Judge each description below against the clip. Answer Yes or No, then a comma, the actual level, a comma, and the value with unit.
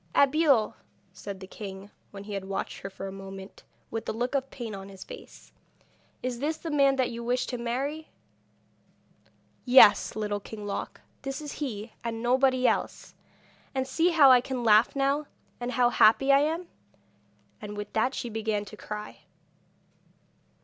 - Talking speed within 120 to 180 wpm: Yes, average, 170 wpm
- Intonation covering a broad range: No, average, 4.6 semitones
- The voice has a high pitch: Yes, high, 240 Hz